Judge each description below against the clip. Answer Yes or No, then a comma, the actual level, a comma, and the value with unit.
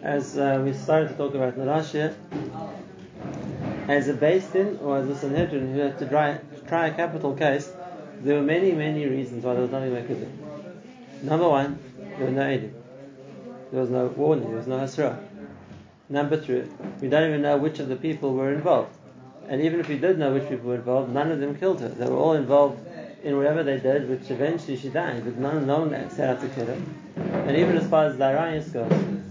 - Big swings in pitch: No, average, 2.8 semitones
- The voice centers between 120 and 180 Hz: Yes, medium, 140 Hz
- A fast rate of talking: Yes, fast, 220 wpm